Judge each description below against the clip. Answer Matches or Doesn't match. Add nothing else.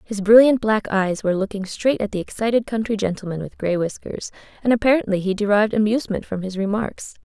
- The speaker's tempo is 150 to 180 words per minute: Doesn't match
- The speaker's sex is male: Doesn't match